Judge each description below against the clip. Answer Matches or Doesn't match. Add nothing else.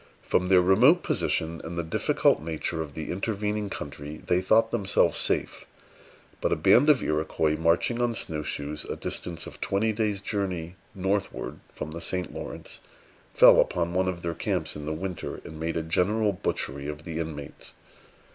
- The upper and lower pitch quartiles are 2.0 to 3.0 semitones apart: Doesn't match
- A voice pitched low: Matches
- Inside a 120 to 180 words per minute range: Matches